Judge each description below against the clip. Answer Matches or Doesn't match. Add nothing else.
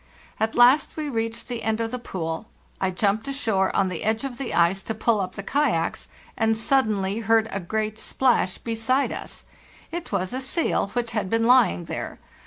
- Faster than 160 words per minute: Matches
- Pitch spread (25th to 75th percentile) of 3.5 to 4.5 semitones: Matches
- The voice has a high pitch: Matches